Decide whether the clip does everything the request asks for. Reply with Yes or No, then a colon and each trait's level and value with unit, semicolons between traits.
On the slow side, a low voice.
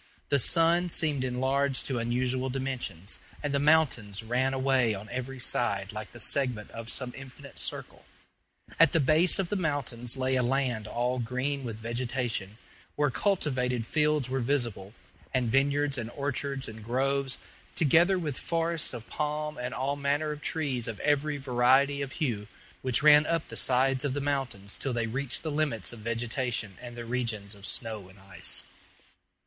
No: average, 170 wpm; low, 130 Hz